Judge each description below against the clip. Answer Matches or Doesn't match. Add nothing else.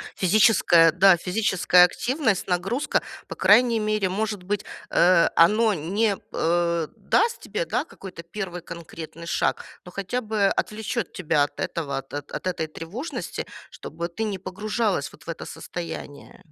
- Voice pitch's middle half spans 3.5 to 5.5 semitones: Matches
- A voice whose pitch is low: Doesn't match